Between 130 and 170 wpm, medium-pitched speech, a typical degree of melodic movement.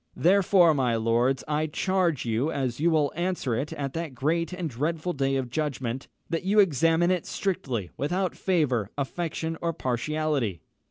Yes: average, 160 wpm; medium, 155 Hz; average, 4.6 semitones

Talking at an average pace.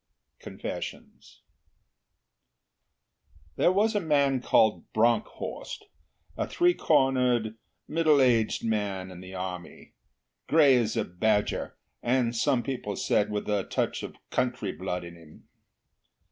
No: slow, 120 wpm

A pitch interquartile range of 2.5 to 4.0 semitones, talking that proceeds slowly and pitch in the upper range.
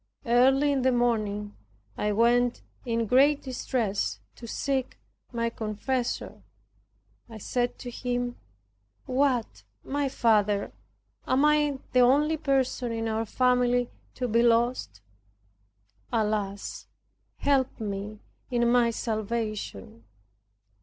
Yes: average, 2.9 semitones; slow, 105 wpm; high, 240 Hz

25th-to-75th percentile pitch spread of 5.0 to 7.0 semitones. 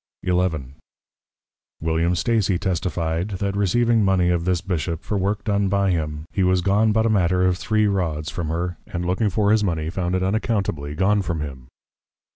No: average, 3.1 semitones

